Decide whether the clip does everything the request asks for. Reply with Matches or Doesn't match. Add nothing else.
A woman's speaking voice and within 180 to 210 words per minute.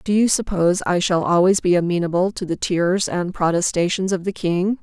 Matches